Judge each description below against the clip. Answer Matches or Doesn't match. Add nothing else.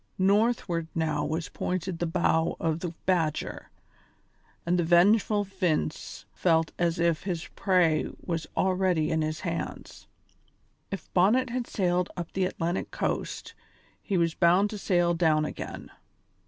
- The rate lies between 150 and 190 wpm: Doesn't match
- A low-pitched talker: Doesn't match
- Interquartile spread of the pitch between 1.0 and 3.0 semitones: Matches